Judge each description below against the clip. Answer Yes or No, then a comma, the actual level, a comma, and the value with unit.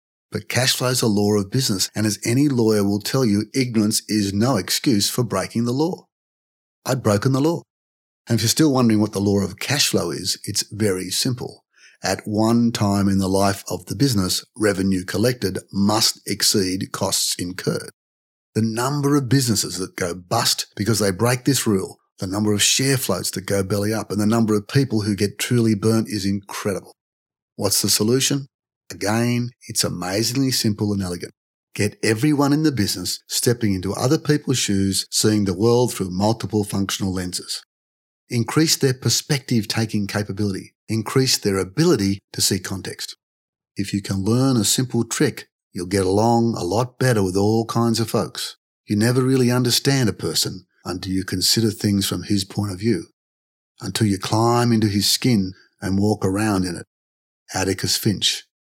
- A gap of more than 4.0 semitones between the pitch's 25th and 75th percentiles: No, average, 3.7 semitones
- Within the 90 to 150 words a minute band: No, average, 175 wpm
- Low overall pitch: Yes, low, 105 Hz